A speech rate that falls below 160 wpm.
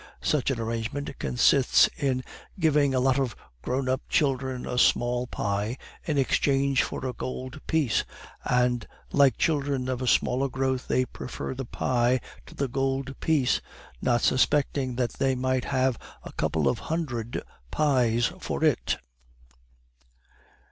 Yes: average, 140 wpm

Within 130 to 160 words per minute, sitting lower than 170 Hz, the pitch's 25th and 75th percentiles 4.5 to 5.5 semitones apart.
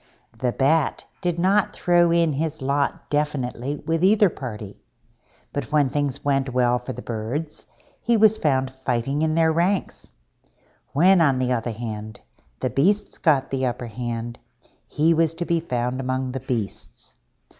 Yes: average, 155 wpm; medium, 140 Hz; average, 4.8 semitones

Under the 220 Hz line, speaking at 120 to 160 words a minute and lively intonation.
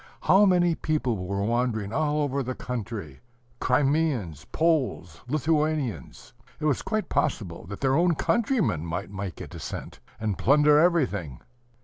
Yes: low, 135 Hz; slow, 135 wpm; wide, 7.5 semitones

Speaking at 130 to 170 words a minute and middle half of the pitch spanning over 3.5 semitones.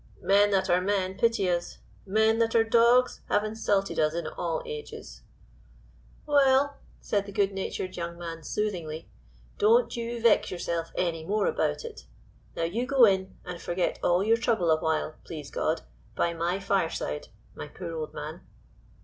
Yes: average, 160 wpm; average, 5.1 semitones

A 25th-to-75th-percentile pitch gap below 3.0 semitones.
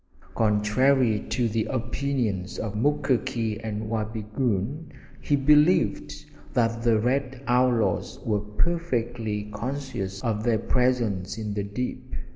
No: average, 3.5 semitones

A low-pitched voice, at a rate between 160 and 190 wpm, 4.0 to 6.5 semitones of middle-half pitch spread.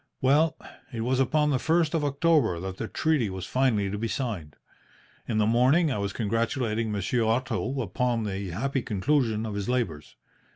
Yes: low, 115 Hz; average, 175 wpm; average, 4.6 semitones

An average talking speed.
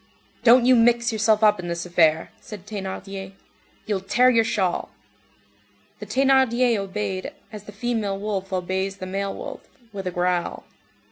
Yes: average, 150 wpm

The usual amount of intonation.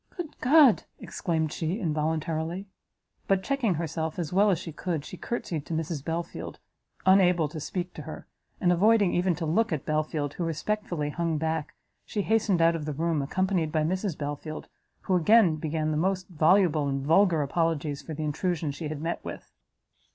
Yes: average, 3.2 semitones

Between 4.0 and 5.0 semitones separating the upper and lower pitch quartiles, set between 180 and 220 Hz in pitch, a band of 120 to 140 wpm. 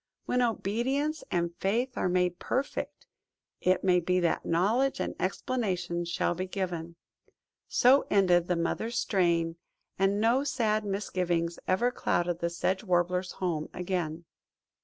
Yes: average, 4.3 semitones; medium, 185 Hz; slow, 135 wpm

